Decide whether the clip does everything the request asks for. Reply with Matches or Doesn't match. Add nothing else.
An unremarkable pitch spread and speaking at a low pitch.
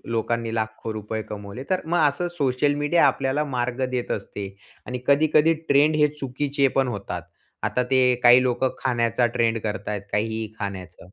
Matches